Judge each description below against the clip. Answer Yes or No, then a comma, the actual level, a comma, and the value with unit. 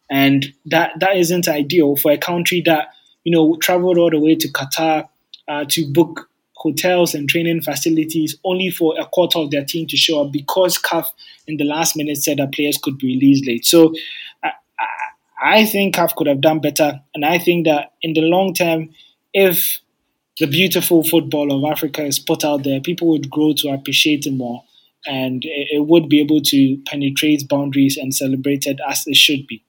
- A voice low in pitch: No, medium, 155 Hz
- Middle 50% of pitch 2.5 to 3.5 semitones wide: Yes, average, 2.9 semitones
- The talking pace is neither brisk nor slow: Yes, average, 195 wpm